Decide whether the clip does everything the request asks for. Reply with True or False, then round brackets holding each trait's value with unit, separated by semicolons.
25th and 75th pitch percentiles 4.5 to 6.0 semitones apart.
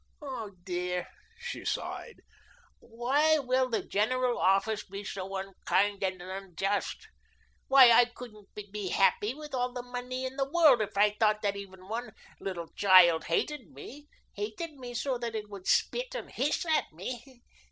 True (4.8 semitones)